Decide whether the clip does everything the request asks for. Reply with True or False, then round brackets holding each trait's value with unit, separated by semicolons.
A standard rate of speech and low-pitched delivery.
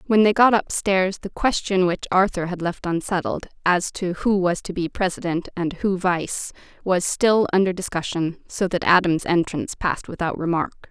False (175 wpm; 180 Hz)